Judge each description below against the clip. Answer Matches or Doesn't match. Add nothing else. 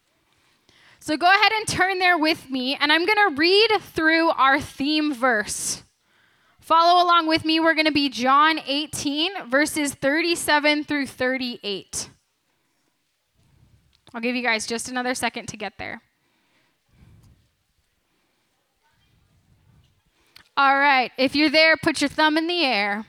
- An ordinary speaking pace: Doesn't match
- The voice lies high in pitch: Matches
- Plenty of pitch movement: Doesn't match